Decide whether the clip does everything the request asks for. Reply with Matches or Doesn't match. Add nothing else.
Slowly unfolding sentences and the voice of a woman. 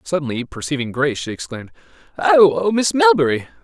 Doesn't match